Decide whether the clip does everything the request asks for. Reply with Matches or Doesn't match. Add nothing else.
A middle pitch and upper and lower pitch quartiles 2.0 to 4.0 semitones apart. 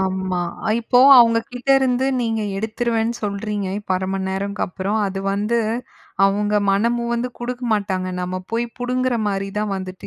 Doesn't match